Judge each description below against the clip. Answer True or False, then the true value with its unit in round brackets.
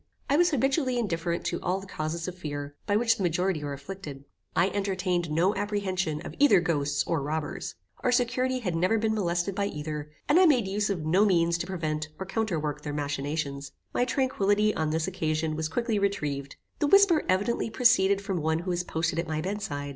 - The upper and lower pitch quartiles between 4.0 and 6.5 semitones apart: True (5.0 semitones)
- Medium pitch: True (180 Hz)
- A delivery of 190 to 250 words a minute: True (200 wpm)